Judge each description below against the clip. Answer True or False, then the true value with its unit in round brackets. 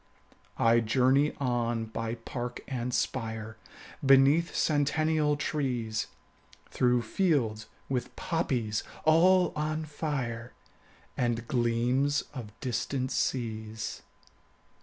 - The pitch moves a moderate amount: True (4.2 semitones)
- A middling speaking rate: False (95 wpm)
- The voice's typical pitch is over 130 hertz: False (125 Hz)